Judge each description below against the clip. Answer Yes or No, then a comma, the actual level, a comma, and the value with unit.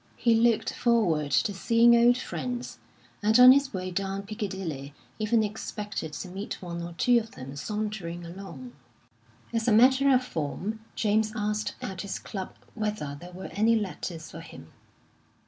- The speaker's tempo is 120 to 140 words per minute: No, average, 160 wpm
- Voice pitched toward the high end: Yes, high, 210 Hz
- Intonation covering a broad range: No, average, 4.6 semitones